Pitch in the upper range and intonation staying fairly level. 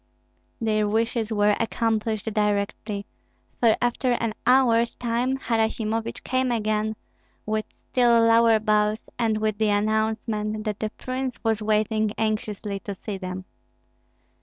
Yes: high, 220 Hz; narrow, 1.4 semitones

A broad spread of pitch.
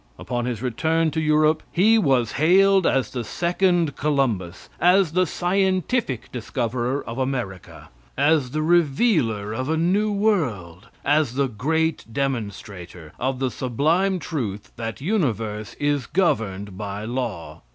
Yes: wide, 6.6 semitones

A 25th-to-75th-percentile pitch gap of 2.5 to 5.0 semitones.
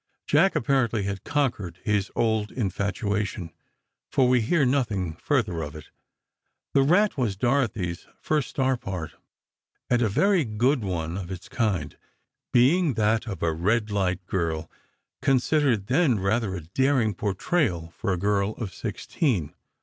No: wide, 5.6 semitones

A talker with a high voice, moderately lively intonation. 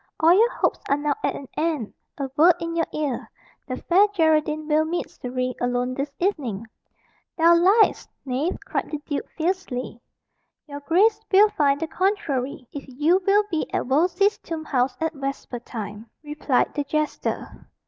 Yes: very high, 305 Hz; average, 4.4 semitones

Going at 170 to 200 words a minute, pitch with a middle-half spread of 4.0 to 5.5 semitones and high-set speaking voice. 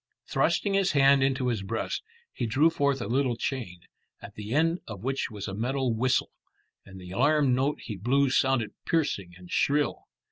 No: average, 180 wpm; average, 4.4 semitones; low, 130 Hz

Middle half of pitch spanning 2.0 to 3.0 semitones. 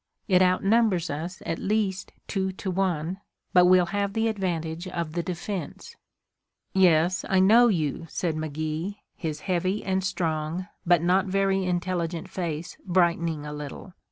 Yes: narrow, 2.6 semitones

